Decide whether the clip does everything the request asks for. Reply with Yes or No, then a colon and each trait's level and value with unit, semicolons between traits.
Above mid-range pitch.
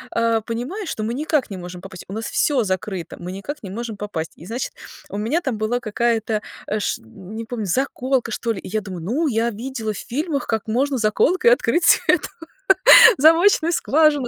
Yes: high, 230 Hz